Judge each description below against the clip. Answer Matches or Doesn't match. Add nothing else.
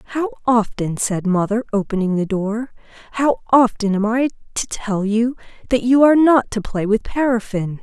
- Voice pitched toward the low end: Doesn't match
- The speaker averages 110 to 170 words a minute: Matches